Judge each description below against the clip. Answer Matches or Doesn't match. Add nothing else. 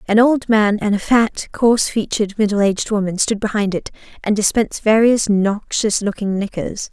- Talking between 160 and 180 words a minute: Matches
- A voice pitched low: Doesn't match